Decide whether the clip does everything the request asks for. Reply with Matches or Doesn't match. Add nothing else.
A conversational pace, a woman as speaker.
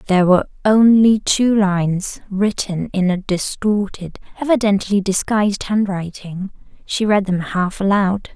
Doesn't match